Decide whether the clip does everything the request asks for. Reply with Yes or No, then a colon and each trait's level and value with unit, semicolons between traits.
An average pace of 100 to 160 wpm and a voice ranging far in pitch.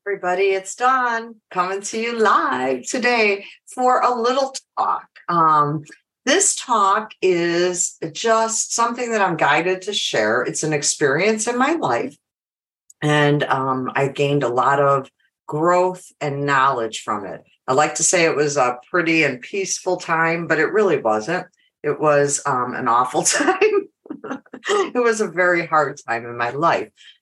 Yes: average, 155 wpm; wide, 7.5 semitones